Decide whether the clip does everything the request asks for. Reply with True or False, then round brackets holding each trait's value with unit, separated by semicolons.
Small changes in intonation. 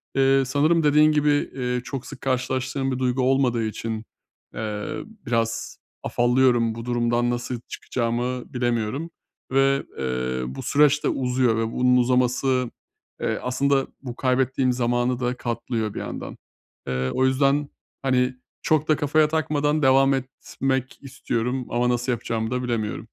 True (2.2 semitones)